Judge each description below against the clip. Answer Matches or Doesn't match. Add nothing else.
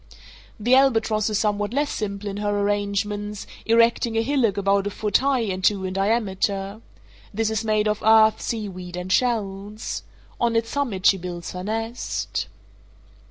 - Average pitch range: Doesn't match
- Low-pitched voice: Doesn't match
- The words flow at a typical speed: Matches